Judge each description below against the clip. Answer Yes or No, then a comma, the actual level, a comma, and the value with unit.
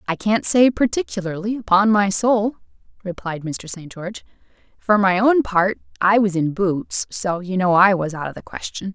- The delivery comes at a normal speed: Yes, average, 190 wpm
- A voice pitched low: No, high, 195 Hz